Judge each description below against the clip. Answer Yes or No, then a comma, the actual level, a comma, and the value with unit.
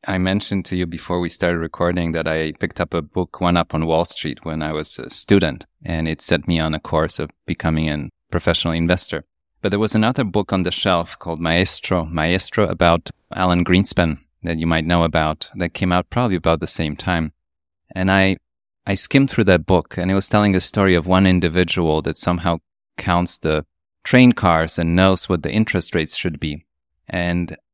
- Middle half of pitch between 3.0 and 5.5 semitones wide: No, narrow, 2.4 semitones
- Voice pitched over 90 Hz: No, very low, 85 Hz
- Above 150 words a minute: Yes, fast, 205 wpm